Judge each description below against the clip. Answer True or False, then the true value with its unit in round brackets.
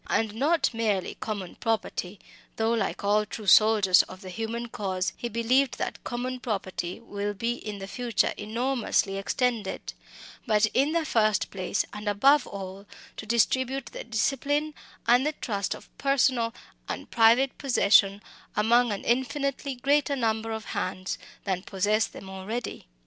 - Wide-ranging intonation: False (3.6 semitones)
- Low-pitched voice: False (225 Hz)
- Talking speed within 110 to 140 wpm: False (150 wpm)